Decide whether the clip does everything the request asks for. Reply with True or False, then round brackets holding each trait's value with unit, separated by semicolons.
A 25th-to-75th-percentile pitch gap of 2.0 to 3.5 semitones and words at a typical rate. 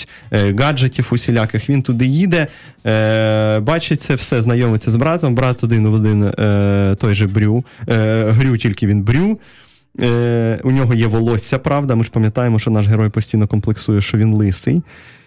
True (3.1 semitones; 145 wpm)